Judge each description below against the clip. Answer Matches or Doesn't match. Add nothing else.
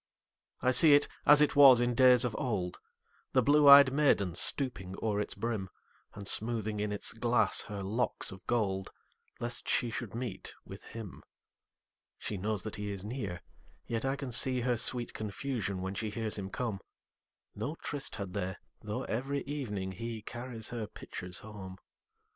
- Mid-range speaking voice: Doesn't match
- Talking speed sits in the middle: Matches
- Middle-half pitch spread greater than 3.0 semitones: Matches